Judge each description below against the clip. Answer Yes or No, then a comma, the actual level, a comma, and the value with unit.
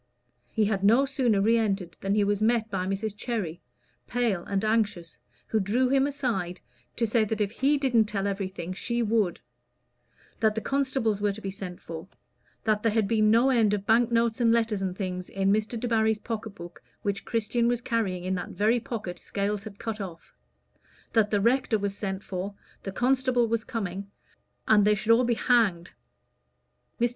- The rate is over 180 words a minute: Yes, average, 190 wpm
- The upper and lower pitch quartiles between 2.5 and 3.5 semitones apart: Yes, average, 2.9 semitones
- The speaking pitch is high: Yes, high, 215 Hz